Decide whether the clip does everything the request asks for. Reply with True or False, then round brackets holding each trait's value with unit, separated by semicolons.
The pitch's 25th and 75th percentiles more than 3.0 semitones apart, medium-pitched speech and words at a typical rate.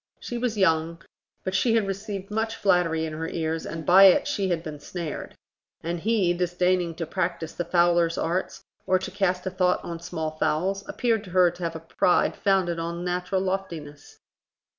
False (2.6 semitones; 180 Hz; 185 wpm)